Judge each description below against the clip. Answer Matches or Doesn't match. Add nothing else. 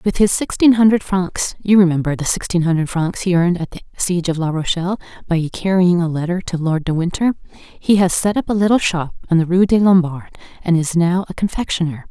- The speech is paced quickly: Matches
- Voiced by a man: Doesn't match